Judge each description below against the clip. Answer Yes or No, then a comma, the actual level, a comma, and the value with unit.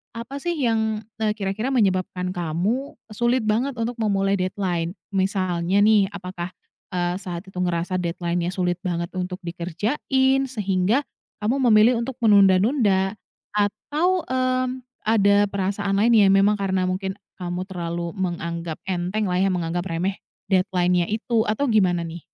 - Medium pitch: No, high, 195 Hz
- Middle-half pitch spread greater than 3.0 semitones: Yes, average, 3.5 semitones